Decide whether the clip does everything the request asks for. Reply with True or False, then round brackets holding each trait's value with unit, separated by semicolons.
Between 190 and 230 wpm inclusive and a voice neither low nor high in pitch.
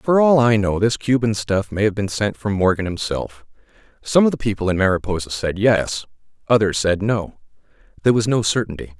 False (195 wpm; 105 Hz)